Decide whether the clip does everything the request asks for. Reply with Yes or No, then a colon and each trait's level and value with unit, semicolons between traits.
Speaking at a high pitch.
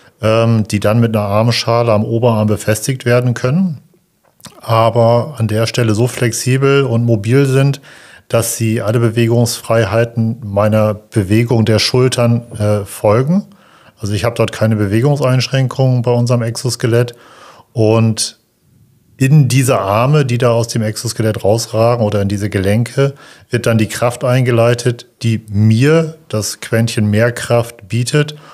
No: low, 115 Hz